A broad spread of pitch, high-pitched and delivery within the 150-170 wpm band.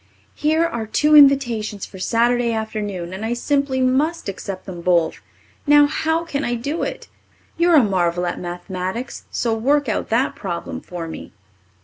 Yes: wide, 7.0 semitones; high, 230 Hz; average, 160 wpm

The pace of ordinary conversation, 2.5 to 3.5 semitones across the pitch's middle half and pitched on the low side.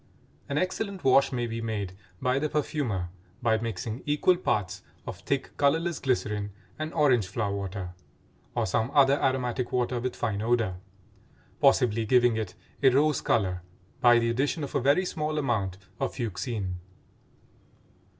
No: average, 150 wpm; average, 4.9 semitones; low, 120 Hz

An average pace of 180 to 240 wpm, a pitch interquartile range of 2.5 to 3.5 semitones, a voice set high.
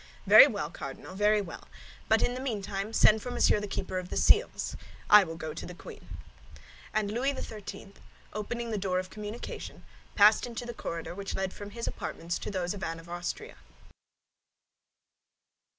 No: average, 165 wpm; average, 2.9 semitones; high, 205 Hz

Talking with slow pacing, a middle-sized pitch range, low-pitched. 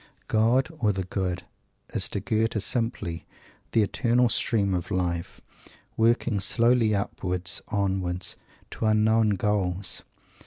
Yes: slow, 115 wpm; average, 3.4 semitones; low, 105 Hz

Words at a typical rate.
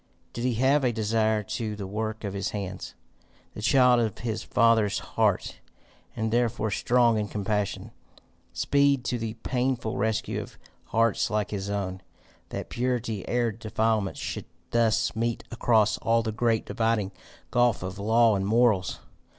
Yes: average, 150 wpm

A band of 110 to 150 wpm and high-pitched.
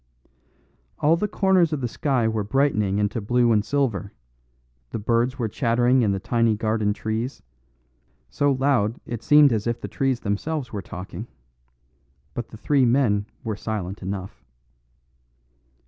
No: average, 145 wpm; low, 115 Hz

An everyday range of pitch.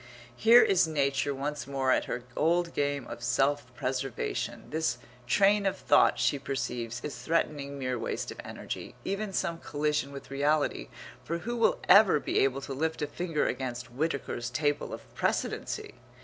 Yes: average, 3.6 semitones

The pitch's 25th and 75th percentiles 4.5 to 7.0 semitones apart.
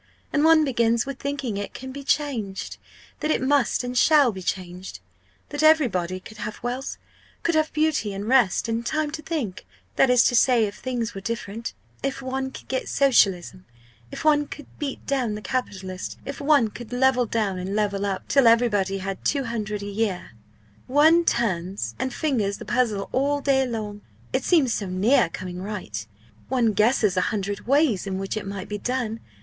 Yes: average, 5.3 semitones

